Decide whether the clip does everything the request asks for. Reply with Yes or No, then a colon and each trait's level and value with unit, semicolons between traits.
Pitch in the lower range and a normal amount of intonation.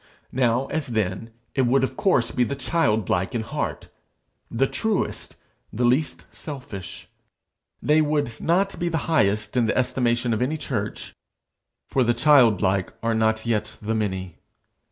Yes: low, 120 Hz; average, 4.2 semitones